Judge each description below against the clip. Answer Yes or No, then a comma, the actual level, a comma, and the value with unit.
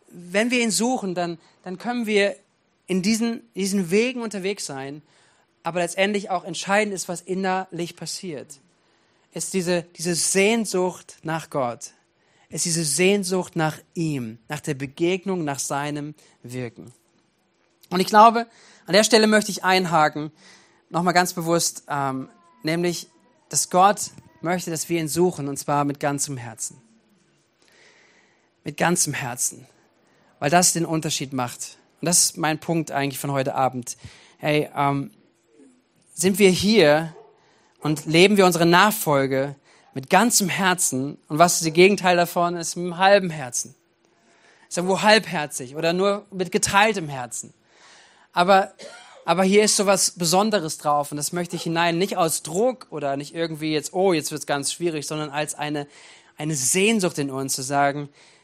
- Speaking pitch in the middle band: Yes, medium, 170 Hz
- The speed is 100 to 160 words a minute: Yes, average, 155 wpm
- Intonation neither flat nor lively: Yes, average, 4.4 semitones